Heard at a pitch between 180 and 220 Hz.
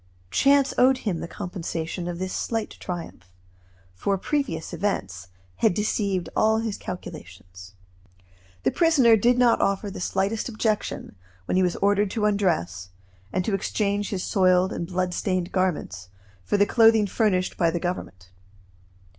Yes: high, 190 Hz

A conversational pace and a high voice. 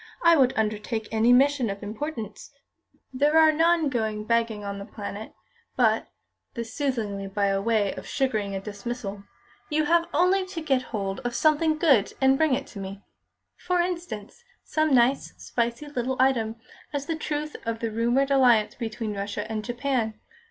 Yes: average, 170 wpm; high, 240 Hz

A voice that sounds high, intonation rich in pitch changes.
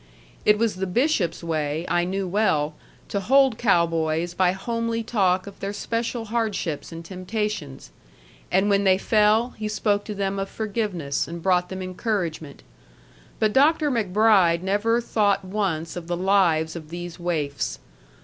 No: high, 195 Hz; average, 4.0 semitones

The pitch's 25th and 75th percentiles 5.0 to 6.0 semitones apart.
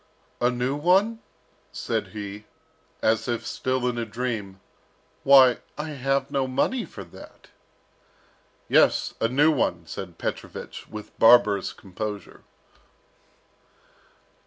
No: average, 4.6 semitones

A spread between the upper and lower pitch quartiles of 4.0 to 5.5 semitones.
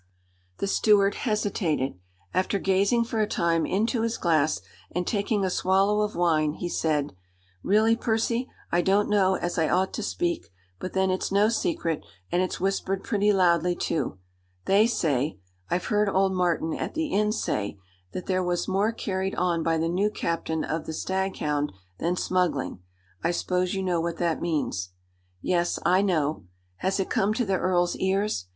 No: average, 3.4 semitones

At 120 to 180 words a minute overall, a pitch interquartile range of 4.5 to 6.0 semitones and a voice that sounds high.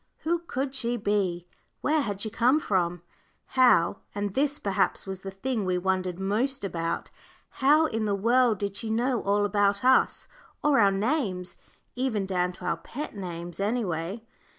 Yes: average, 170 wpm; average, 5.0 semitones; high, 205 Hz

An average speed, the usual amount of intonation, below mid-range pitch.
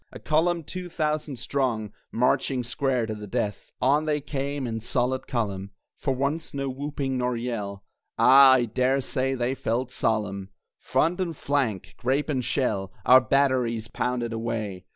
Yes: average, 155 wpm; average, 3.5 semitones; low, 130 Hz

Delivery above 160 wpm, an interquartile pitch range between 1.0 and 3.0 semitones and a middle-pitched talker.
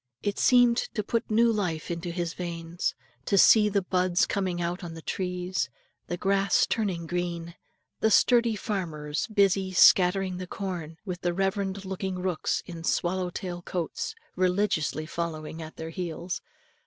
No: average, 155 wpm; narrow, 2.5 semitones; medium, 180 Hz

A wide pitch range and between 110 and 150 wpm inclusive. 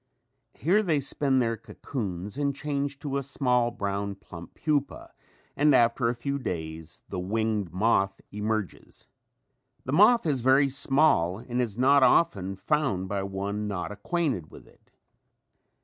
Yes: wide, 6.1 semitones; average, 145 wpm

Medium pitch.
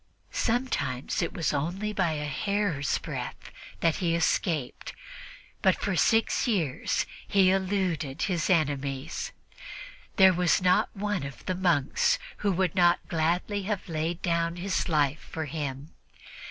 Yes: medium, 170 Hz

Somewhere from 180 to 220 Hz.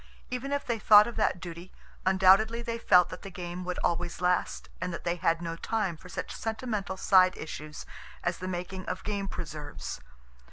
Yes: medium, 185 Hz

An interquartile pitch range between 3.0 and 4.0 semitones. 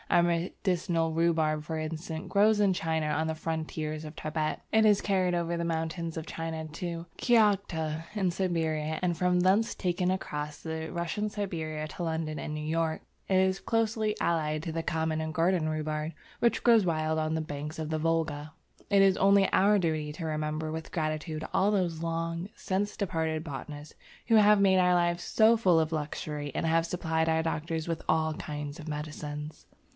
No: narrow, 2.6 semitones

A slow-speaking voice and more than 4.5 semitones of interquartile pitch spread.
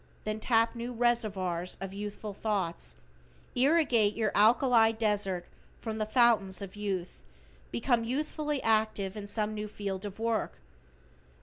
No: slow, 130 wpm; average, 2.7 semitones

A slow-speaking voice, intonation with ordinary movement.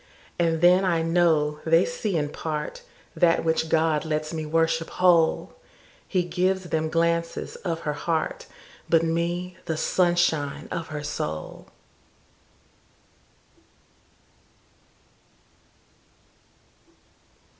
No: slow, 90 wpm; narrow, 1.7 semitones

